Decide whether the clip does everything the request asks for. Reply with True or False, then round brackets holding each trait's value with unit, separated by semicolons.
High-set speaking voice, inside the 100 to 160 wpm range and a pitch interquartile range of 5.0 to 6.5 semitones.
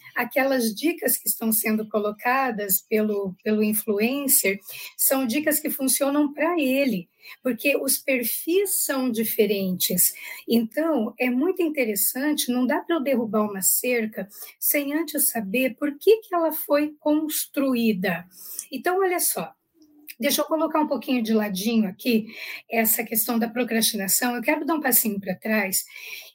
True (255 Hz; 140 wpm; 5.4 semitones)